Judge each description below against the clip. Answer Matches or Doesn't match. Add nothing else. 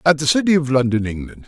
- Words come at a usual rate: Doesn't match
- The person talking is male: Matches